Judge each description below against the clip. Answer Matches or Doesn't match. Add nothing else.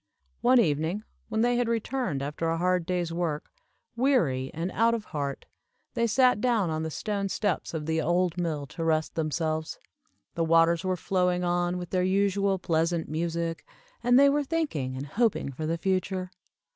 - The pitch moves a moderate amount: Matches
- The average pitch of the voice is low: Doesn't match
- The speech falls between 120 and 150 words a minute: Doesn't match